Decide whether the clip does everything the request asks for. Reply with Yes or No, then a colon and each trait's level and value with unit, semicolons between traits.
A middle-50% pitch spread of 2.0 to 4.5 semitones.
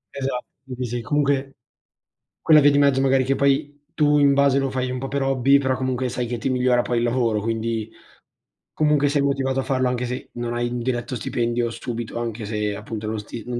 Yes: narrow, 2.5 semitones